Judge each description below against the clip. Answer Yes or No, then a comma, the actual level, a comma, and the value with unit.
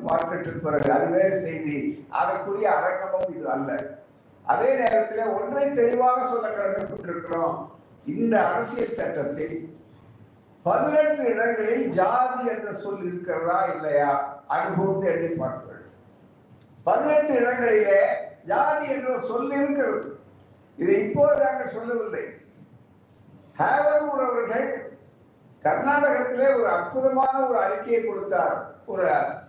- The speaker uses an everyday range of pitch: No, wide, 7.7 semitones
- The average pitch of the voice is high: Yes, high, 230 Hz